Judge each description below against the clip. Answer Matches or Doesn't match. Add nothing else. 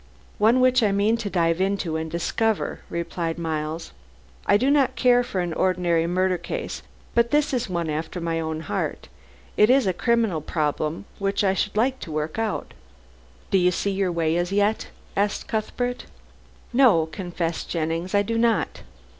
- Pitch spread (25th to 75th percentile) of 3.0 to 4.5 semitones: Doesn't match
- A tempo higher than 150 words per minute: Matches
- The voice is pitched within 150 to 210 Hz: Matches